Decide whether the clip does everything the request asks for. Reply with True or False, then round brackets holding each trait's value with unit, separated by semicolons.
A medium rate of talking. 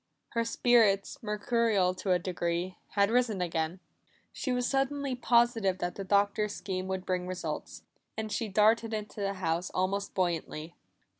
True (150 wpm)